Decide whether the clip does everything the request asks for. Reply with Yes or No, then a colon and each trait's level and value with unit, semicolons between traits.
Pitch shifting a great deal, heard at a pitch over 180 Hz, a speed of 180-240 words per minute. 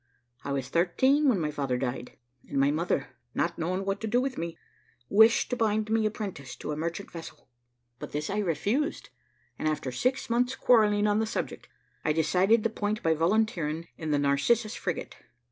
Yes: wide, 6.3 semitones; high, 190 Hz; average, 185 wpm